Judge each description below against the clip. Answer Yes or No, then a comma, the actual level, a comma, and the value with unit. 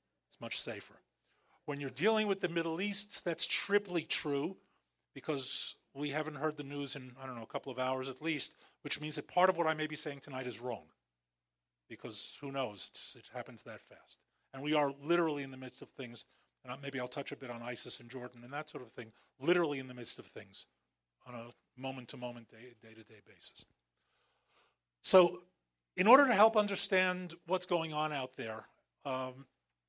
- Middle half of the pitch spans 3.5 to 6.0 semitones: Yes, average, 4.7 semitones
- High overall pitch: No, medium, 140 Hz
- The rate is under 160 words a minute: No, fast, 205 wpm